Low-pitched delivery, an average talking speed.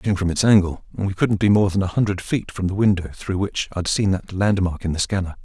No: very low, 95 Hz; fast, 265 wpm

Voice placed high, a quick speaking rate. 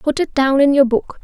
Yes: very high, 275 Hz; fast, 290 wpm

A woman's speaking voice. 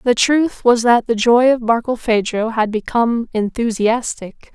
Yes: female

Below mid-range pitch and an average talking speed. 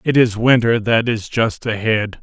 Yes: low, 115 Hz; average, 190 wpm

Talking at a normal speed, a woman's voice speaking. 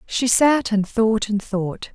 Yes: average, 185 wpm; female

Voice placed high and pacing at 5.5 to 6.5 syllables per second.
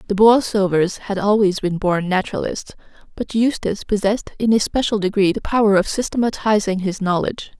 Yes: high, 205 Hz; 5.7 syllables/s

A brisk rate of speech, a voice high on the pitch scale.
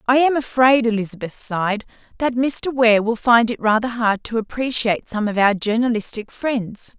No: average, 170 wpm; high, 230 Hz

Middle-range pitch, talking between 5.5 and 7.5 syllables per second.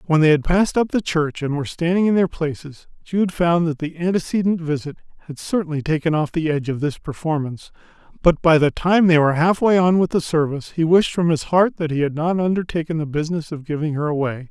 Yes: medium, 160 Hz; 6.1 syllables/s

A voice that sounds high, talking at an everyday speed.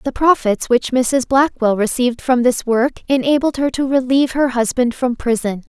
Yes: very high, 250 Hz; average, 175 wpm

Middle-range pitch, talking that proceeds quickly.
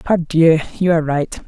No: medium, 160 Hz; average, 165 wpm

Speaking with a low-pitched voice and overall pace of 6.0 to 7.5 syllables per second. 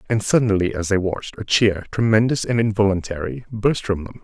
No: low, 105 Hz; 5.6 syllables/s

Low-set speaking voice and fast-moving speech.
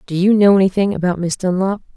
No: high, 190 Hz; fast, 215 wpm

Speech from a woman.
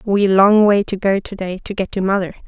Yes: female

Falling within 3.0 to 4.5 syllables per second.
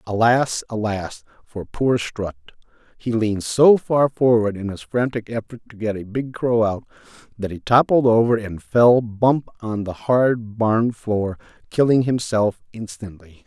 Yes: 4.1 syllables/s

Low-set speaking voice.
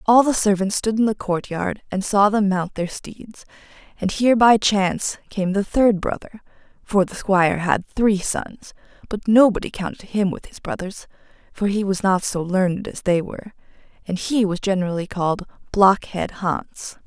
No: high, 200 Hz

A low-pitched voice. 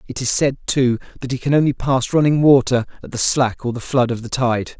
Yes: low, 130 Hz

